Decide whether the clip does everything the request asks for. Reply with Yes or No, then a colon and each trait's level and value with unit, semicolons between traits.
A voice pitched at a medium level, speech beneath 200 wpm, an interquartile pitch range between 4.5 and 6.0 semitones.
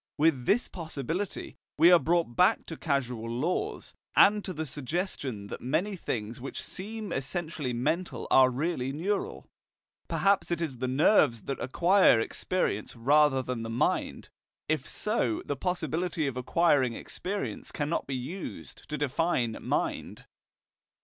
Yes: medium, 150 Hz; average, 140 wpm; wide, 5.6 semitones